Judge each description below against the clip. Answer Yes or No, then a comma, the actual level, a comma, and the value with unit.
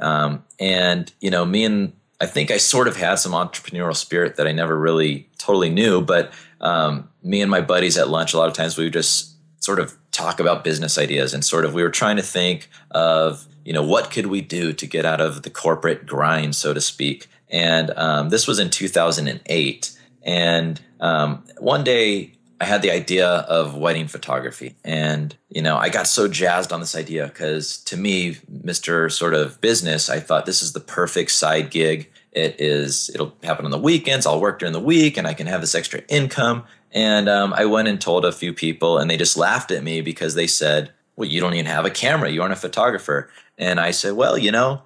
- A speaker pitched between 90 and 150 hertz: No, very low, 80 Hz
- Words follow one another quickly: Yes, fast, 220 wpm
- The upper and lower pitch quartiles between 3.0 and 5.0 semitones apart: Yes, average, 4.0 semitones